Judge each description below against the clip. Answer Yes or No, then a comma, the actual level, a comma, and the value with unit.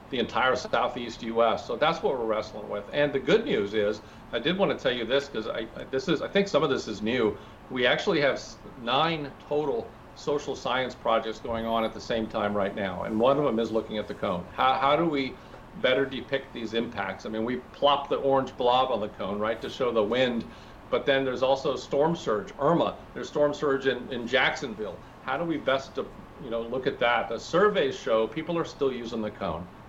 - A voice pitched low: Yes, low, 120 Hz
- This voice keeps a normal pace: No, fast, 225 wpm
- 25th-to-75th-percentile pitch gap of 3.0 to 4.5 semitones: Yes, average, 3.7 semitones